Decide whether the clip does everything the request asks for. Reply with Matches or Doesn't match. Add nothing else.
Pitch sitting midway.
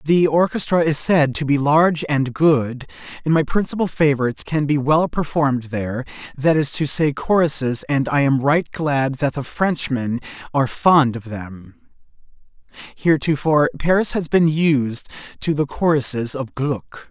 Matches